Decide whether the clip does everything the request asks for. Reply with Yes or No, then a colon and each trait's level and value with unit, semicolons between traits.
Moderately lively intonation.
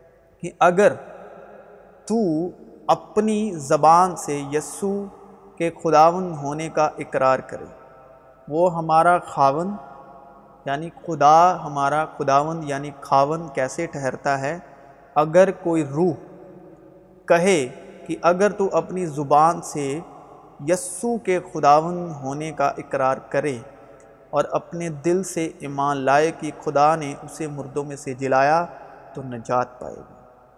Yes: average, 3.8 semitones